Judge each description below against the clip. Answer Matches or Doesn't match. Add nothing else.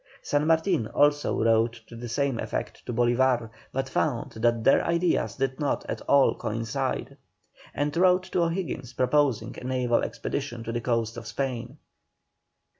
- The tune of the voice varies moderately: Matches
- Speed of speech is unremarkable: Matches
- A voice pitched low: Matches